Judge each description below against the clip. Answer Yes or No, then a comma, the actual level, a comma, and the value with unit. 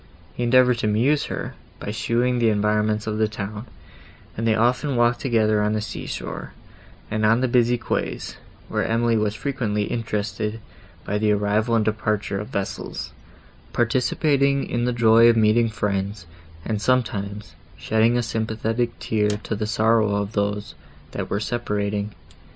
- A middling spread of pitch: No, narrow, 2.2 semitones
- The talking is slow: No, average, 155 wpm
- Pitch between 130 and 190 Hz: No, low, 110 Hz